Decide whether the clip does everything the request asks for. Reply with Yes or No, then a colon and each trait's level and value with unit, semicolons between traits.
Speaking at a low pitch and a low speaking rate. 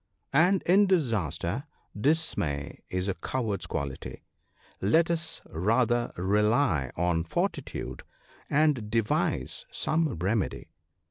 Yes: low, 110 Hz; slow, 105 wpm